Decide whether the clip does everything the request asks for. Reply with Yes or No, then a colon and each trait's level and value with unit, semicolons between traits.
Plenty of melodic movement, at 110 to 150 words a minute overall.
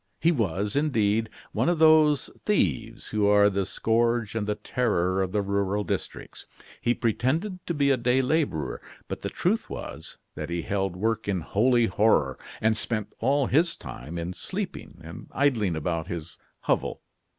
No: wide, 5.9 semitones; average, 165 wpm